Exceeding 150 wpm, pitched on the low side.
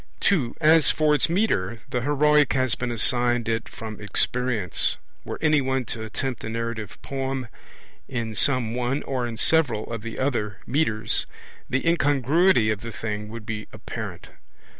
Yes: average, 160 wpm; low, 125 Hz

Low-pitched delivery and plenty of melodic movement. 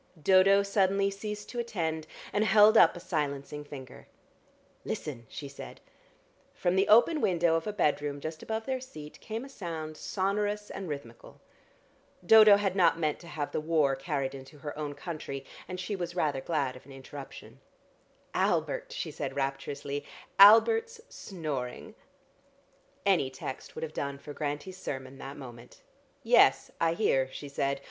No: medium, 160 Hz; wide, 5.9 semitones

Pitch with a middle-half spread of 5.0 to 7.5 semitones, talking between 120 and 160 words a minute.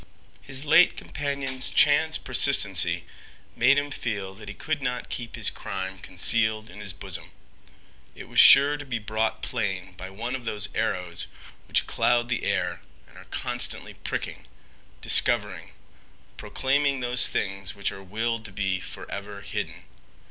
Yes: average, 5.3 semitones; average, 150 wpm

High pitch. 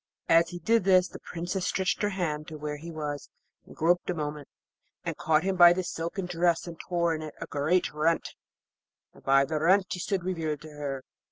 No: medium, 165 Hz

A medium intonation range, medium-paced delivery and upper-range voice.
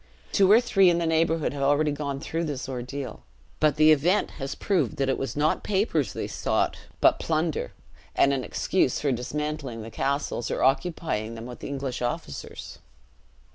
No: average, 3.3 semitones; average, 175 wpm; medium, 145 Hz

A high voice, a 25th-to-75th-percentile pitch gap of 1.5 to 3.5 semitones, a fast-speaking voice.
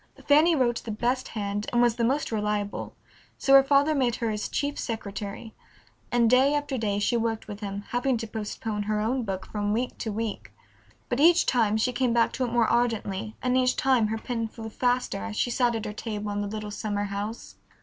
Yes: high, 225 Hz; average, 3.2 semitones; fast, 215 wpm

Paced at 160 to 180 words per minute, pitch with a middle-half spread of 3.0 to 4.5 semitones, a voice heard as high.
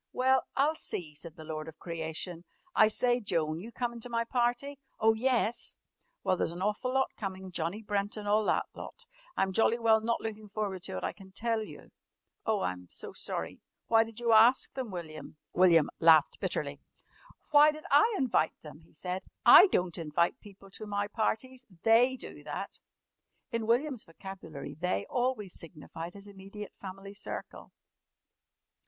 No: average, 170 wpm; wide, 5.5 semitones; high, 205 Hz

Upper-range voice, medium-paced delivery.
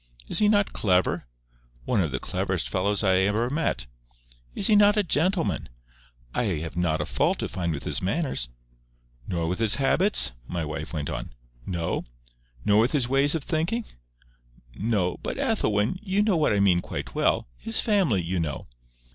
No: low, 105 Hz; average, 170 wpm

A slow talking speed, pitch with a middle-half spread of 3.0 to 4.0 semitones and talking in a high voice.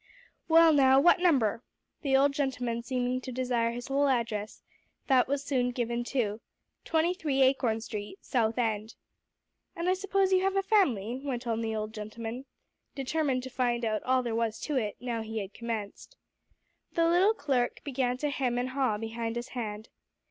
No: average, 175 wpm; average, 3.6 semitones; very high, 250 Hz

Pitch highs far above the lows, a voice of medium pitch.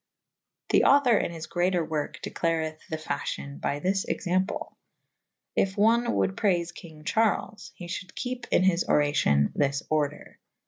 No: average, 4.0 semitones; medium, 170 Hz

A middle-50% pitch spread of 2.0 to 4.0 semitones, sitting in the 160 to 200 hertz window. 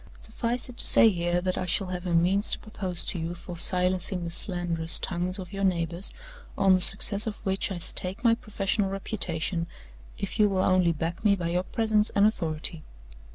Yes: narrow, 2.6 semitones; medium, 185 Hz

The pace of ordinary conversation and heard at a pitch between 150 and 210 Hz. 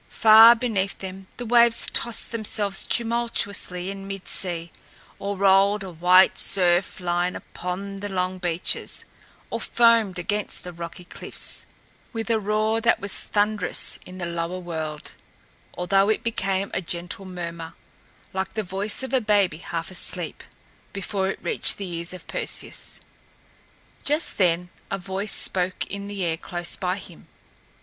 Yes: average, 150 wpm; high, 190 Hz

